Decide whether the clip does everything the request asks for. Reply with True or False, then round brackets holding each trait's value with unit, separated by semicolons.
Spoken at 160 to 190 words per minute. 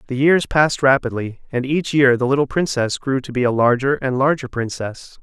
False (205 wpm)